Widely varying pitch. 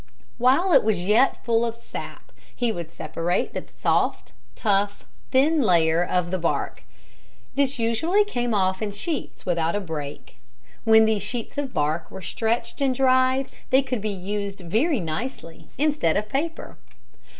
Yes: wide, 6.6 semitones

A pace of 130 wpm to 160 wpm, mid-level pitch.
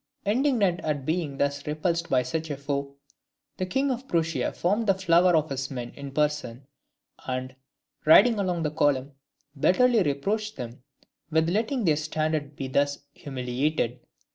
Yes: average, 150 wpm; medium, 155 Hz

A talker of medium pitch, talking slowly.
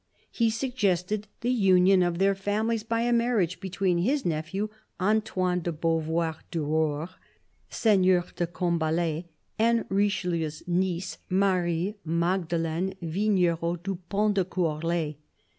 Yes: medium, 180 Hz; slow, 125 wpm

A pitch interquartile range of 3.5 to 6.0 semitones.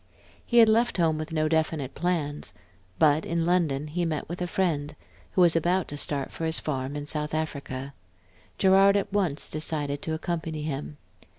No: average, 3.0 semitones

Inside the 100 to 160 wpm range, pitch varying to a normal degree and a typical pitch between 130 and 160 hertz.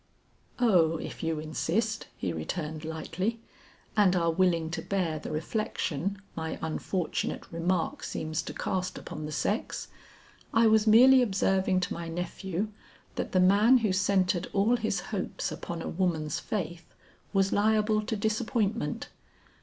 No: average, 140 wpm; average, 4.5 semitones; medium, 185 Hz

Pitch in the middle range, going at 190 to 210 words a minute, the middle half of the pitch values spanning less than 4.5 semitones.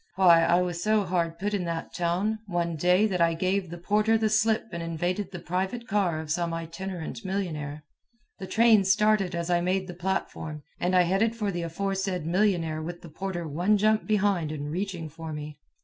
Yes: medium, 180 Hz; average, 195 wpm; average, 3.0 semitones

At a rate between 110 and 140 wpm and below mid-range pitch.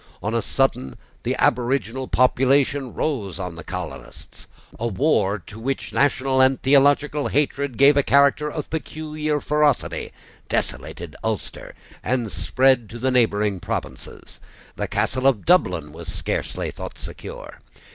Yes: slow, 135 wpm; low, 130 Hz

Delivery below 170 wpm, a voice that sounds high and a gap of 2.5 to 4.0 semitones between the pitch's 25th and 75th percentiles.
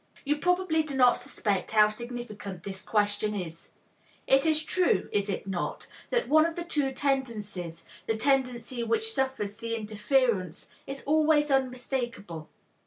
No: average, 145 wpm; high, 245 Hz; wide, 5.6 semitones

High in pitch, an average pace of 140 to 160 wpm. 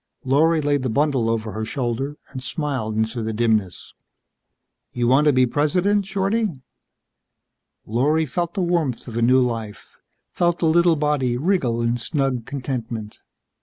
No: low, 130 Hz; average, 150 wpm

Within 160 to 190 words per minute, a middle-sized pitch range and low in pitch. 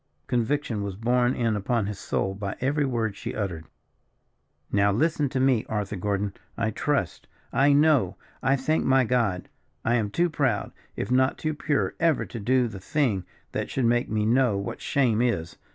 Yes: average, 180 wpm; average, 4.6 semitones; low, 120 Hz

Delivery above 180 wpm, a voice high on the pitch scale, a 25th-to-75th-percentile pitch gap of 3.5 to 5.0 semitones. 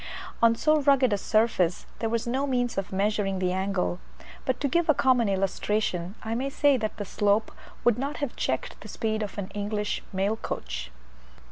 Yes: average, 190 wpm; high, 215 Hz; average, 4.3 semitones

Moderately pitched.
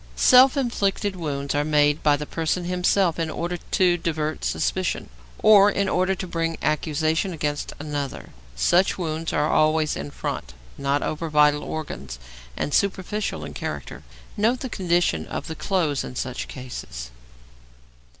Yes: medium, 160 Hz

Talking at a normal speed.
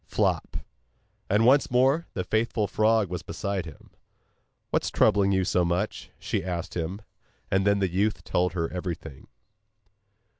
Yes: average, 150 wpm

